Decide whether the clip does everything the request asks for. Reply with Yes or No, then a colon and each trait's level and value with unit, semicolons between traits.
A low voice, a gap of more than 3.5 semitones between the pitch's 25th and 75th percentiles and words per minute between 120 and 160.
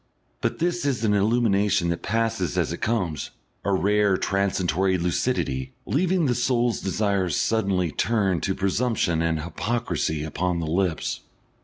Yes: low, 100 Hz; average, 4.7 semitones; average, 140 wpm